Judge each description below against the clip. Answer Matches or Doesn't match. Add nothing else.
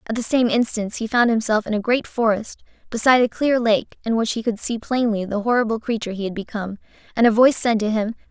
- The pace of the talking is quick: Matches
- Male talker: Doesn't match